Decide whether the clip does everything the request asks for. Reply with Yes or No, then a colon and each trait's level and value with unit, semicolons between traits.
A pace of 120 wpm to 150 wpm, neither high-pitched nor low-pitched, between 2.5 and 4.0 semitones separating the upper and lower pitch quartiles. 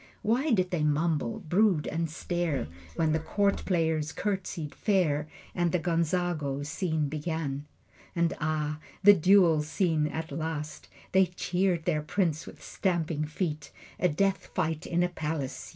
Yes: average, 145 wpm; medium, 165 Hz; average, 3.0 semitones